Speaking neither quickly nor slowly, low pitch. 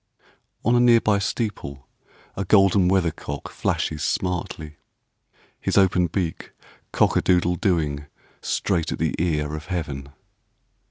No: slow, 130 wpm; very low, 90 Hz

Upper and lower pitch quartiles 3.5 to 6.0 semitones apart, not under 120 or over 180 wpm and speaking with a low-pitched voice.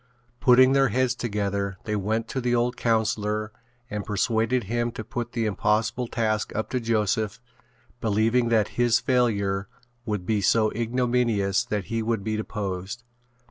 No: narrow, 2.4 semitones; average, 150 wpm; low, 110 Hz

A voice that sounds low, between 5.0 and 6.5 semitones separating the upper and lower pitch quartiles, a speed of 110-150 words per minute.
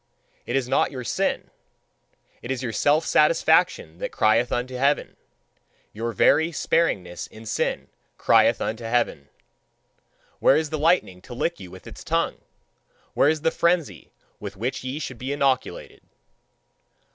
Yes: low, 130 Hz; average, 5.3 semitones; average, 145 wpm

